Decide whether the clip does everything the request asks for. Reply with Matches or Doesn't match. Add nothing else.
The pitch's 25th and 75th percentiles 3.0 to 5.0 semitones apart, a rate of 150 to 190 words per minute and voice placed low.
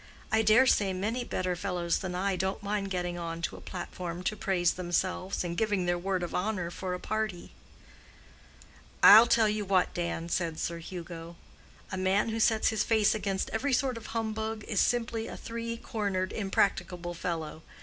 Doesn't match